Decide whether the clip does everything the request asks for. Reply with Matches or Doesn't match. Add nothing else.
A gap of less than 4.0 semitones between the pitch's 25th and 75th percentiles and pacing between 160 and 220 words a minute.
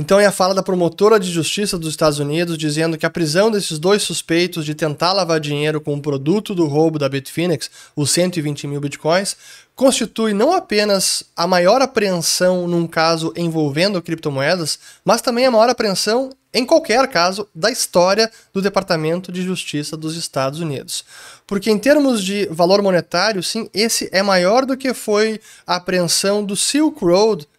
Doesn't match